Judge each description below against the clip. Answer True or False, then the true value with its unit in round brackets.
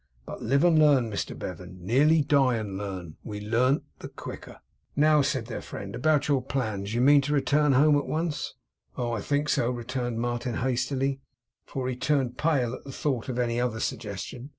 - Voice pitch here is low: True (125 Hz)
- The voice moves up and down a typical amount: True (3.7 semitones)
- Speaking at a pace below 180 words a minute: False (190 wpm)